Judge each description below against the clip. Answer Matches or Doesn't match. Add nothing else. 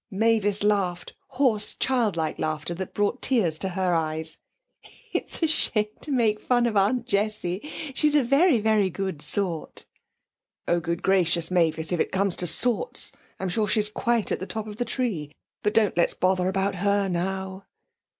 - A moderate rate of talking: Matches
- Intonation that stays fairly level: Doesn't match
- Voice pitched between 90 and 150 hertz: Doesn't match